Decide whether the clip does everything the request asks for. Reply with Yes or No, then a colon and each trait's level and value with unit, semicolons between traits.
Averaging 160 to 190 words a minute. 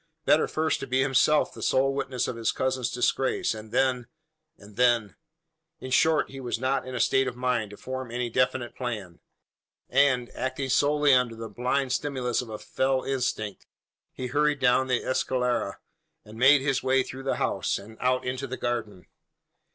Yes: average, 180 wpm